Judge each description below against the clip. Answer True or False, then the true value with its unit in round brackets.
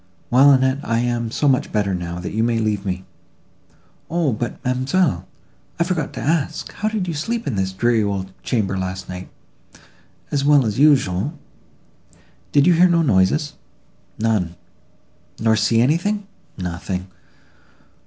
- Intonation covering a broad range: True (7.4 semitones)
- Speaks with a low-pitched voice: True (120 Hz)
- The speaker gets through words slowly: True (130 wpm)